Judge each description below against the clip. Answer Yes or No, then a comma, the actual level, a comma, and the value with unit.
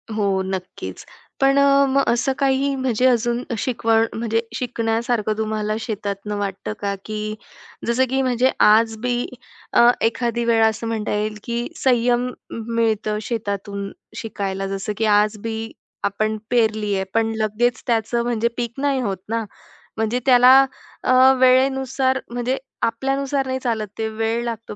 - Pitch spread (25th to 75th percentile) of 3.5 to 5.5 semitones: No, narrow, 2.5 semitones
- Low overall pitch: No, high, 230 Hz